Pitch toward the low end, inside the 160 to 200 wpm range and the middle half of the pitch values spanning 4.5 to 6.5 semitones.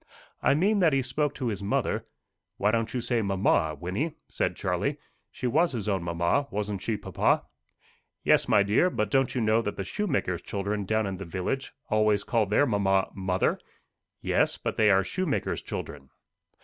Yes: low, 105 Hz; average, 185 wpm; average, 4.8 semitones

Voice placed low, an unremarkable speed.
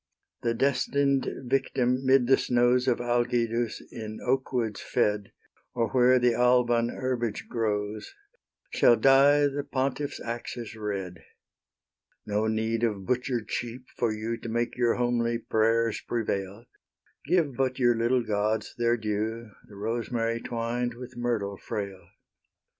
No: low, 120 Hz; slow, 130 wpm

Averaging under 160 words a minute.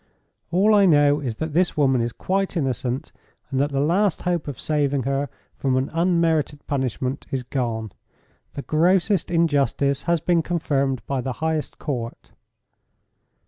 Yes: average, 150 wpm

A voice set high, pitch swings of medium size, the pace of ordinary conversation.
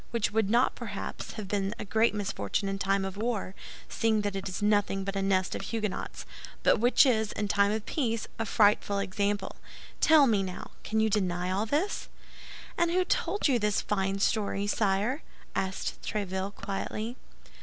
No: high, 205 Hz; narrow, 2.3 semitones; average, 175 wpm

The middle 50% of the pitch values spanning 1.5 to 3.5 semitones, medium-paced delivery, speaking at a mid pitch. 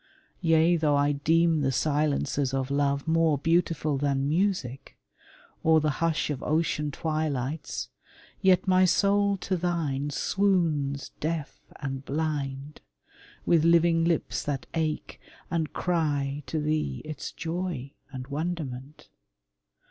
No: average, 3.0 semitones; slow, 120 wpm; medium, 155 Hz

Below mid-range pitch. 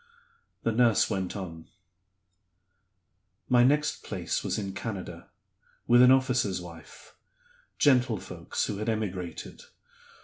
Yes: low, 110 Hz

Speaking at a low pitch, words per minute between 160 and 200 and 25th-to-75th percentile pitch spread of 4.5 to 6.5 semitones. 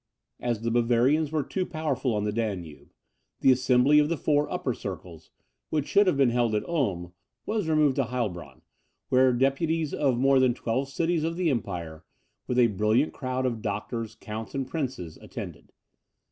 Yes: low, 125 Hz; average, 175 wpm; average, 5.1 semitones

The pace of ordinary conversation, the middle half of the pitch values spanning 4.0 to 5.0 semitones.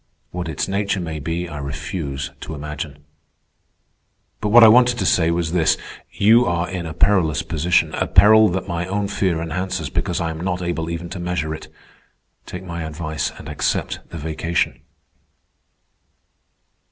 No: average, 160 wpm; average, 3.0 semitones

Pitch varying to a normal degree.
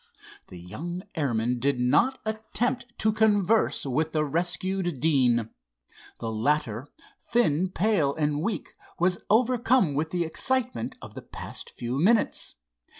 No: wide, 8.1 semitones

